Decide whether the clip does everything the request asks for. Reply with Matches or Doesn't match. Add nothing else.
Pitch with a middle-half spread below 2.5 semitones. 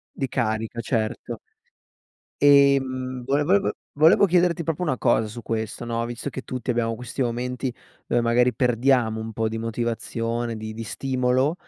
Doesn't match